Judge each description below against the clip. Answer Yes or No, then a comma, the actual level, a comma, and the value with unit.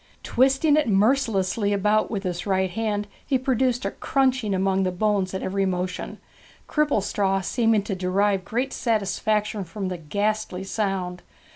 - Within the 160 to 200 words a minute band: No, average, 145 wpm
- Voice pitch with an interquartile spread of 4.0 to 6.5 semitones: No, average, 3.1 semitones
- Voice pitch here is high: Yes, high, 205 Hz